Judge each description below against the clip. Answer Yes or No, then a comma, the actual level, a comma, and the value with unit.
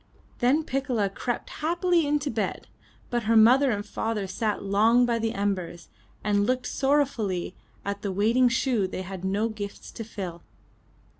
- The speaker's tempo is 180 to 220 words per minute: No, average, 160 wpm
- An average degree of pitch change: Yes, average, 4.1 semitones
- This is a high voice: Yes, high, 220 Hz